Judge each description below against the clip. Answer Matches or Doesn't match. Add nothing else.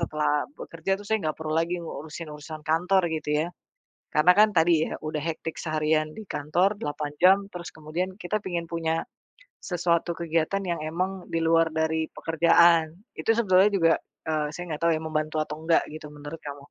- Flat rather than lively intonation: Matches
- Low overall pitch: Doesn't match